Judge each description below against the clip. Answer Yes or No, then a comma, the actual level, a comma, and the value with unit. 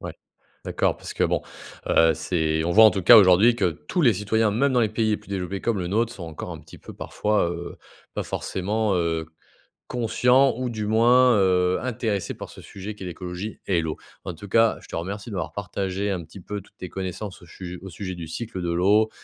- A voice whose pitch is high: No, low, 100 Hz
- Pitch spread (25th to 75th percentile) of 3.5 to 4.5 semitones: Yes, average, 3.8 semitones